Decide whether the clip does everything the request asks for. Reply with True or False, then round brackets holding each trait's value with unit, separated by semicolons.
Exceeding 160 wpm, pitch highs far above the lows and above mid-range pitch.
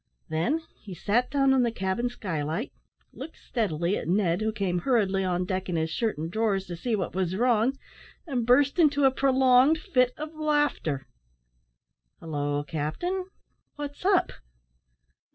False (155 wpm; 7.3 semitones; 220 Hz)